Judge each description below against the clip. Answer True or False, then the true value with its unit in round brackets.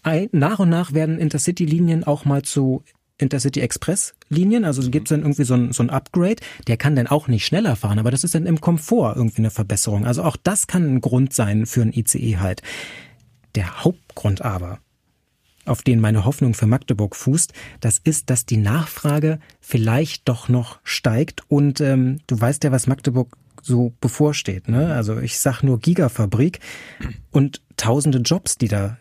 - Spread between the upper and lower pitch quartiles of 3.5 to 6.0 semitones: True (4.5 semitones)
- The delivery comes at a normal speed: True (180 wpm)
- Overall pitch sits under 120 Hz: False (130 Hz)